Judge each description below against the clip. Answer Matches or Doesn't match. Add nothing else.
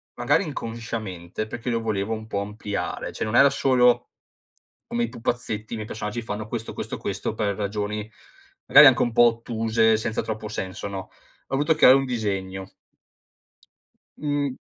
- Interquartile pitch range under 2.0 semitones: Doesn't match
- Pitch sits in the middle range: Doesn't match